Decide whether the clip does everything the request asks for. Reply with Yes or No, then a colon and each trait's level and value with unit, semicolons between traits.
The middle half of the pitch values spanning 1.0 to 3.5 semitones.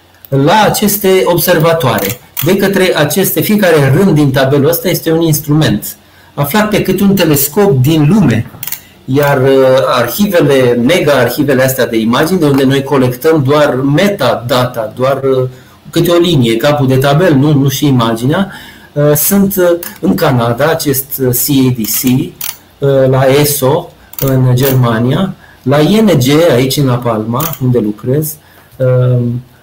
No: average, 4.3 semitones